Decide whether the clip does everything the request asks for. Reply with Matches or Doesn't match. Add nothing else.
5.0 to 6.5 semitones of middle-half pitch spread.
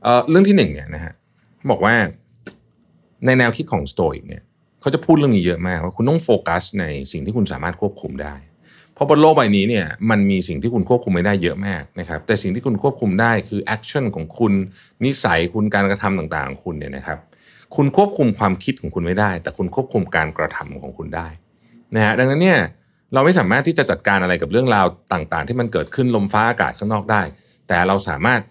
Matches